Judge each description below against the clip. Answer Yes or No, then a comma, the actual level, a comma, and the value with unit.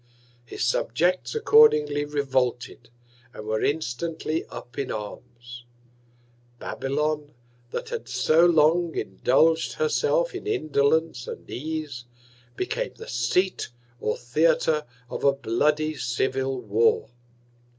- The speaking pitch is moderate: Yes, medium, 150 Hz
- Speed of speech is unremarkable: No, slow, 105 wpm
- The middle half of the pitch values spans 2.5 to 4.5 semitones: No, average, 4.9 semitones